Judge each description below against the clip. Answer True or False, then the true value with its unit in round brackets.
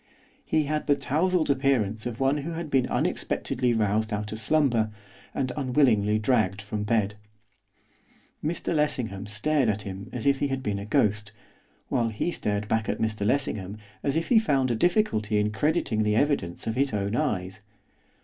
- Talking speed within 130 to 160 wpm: False (175 wpm)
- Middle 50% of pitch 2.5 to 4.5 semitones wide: False (5.1 semitones)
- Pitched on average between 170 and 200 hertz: False (115 Hz)